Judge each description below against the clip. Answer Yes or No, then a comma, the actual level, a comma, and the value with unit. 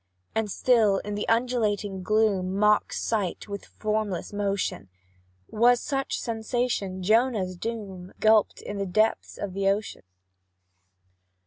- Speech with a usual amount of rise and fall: No, narrow, 2.3 semitones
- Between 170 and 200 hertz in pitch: No, high, 210 Hz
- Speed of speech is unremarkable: No, slow, 110 wpm